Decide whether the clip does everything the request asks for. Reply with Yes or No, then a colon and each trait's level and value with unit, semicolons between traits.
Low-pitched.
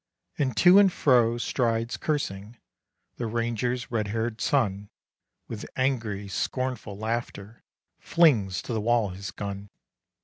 Yes: low, 115 Hz